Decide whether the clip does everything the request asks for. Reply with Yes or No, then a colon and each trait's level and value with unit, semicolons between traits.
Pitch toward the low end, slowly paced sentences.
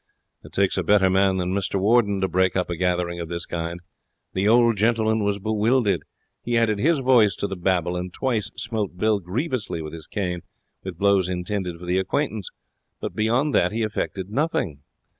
No: low, 100 Hz; average, 190 wpm